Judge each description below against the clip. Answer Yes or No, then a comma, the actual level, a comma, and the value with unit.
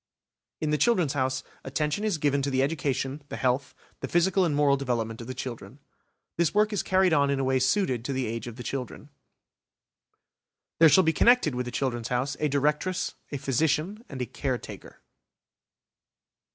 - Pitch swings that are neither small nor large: Yes, average, 3.7 semitones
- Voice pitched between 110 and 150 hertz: Yes, medium, 140 Hz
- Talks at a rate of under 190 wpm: Yes, average, 180 wpm